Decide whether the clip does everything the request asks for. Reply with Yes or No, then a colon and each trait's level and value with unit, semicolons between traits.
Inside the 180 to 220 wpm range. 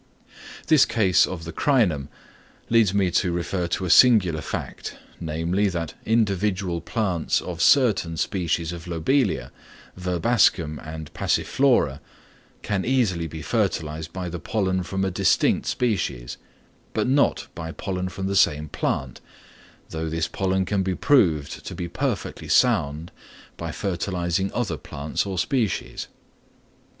No: slow, 135 wpm